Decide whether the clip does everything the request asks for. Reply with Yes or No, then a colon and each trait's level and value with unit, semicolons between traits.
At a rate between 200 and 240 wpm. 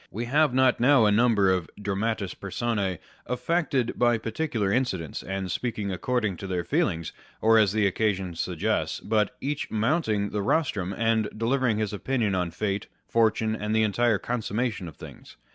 No: average, 160 wpm